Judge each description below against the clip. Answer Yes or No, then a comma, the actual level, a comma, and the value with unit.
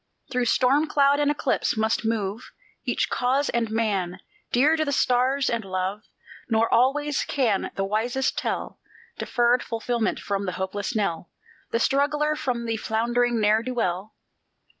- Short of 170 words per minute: Yes, average, 150 wpm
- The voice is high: Yes, high, 235 Hz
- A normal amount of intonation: Yes, average, 3.9 semitones